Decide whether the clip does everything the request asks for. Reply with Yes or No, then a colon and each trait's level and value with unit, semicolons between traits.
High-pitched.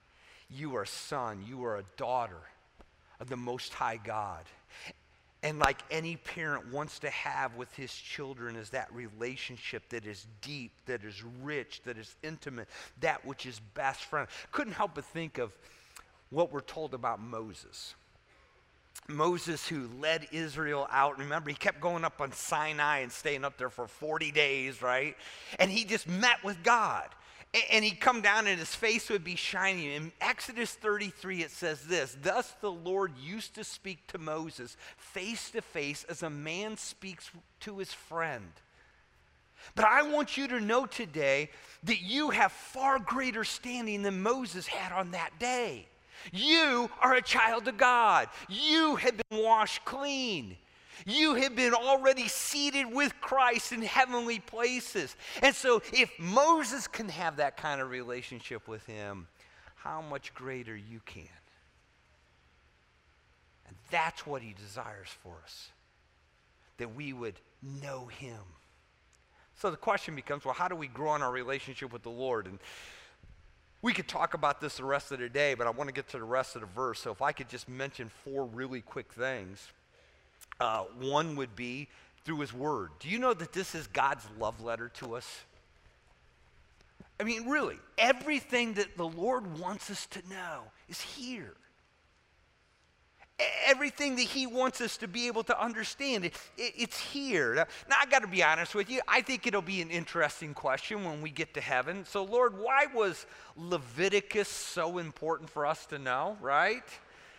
No: medium, 160 Hz